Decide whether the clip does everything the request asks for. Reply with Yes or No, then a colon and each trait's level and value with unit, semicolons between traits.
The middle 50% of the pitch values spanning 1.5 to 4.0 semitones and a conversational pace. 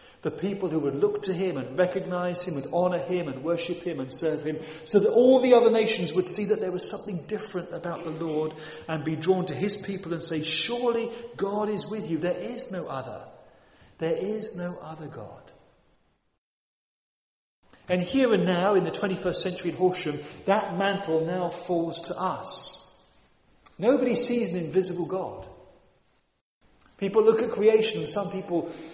Yes: average, 3.7 semitones; average, 175 wpm